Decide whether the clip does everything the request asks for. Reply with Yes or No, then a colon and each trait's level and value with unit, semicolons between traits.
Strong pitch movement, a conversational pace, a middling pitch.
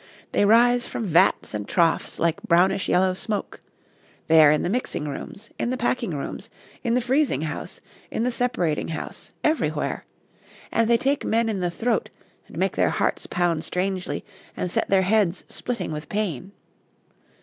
No: wide, 5.7 semitones; average, 170 wpm; high, 195 Hz